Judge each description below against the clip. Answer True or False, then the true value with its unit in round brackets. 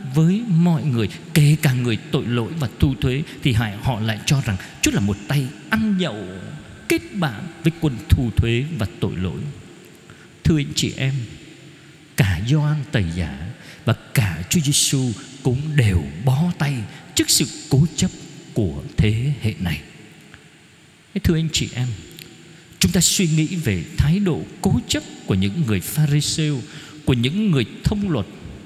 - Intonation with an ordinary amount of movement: False (6.2 semitones)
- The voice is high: False (140 Hz)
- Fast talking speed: False (165 wpm)